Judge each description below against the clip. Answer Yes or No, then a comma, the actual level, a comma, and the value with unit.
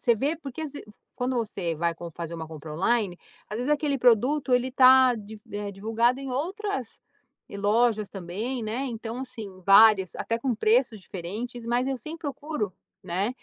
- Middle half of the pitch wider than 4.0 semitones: Yes, average, 4.5 semitones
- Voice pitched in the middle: No, high, 230 Hz